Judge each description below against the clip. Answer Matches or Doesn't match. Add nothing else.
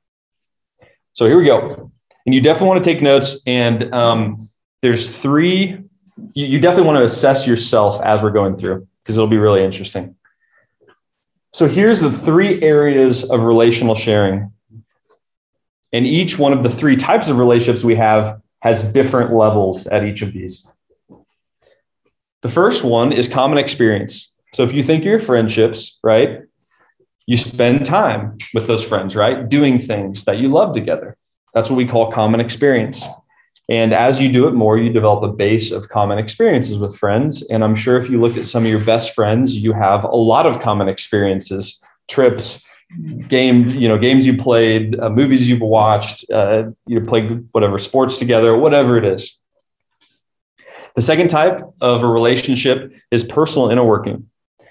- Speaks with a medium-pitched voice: Doesn't match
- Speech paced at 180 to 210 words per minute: Doesn't match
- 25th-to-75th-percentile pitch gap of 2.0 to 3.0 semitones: Doesn't match